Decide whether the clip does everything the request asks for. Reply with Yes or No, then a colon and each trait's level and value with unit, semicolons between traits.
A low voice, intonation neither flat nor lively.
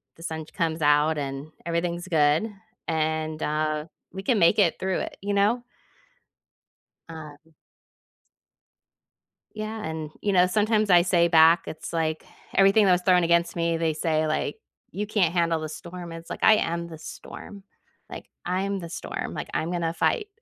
No: medium, 170 Hz; average, 3.1 semitones